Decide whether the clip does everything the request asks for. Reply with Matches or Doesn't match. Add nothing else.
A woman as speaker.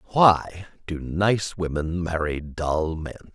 Doesn't match